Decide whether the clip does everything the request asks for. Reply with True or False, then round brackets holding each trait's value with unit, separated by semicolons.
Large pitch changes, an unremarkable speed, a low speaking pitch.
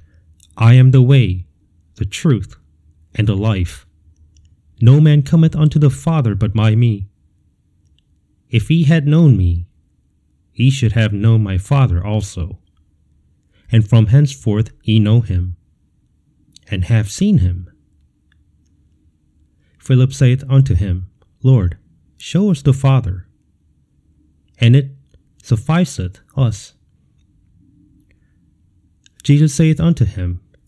False (8.1 semitones; 115 wpm; 95 Hz)